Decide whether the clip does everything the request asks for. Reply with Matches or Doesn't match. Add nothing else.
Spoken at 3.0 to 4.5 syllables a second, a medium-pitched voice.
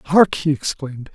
Doesn't match